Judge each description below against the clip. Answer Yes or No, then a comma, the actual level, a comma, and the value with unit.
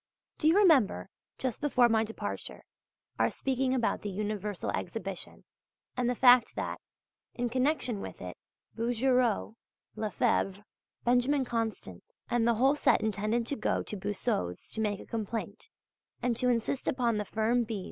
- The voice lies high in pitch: Yes, high, 230 Hz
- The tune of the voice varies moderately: Yes, average, 3.1 semitones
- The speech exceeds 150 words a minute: No, average, 145 wpm